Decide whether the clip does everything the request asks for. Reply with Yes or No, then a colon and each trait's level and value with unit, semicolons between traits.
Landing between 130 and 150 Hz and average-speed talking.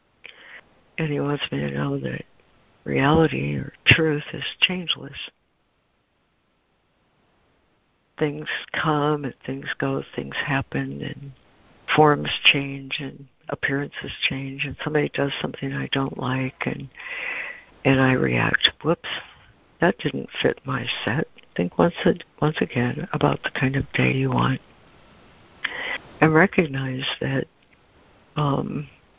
No: low, 135 Hz; slow, 120 wpm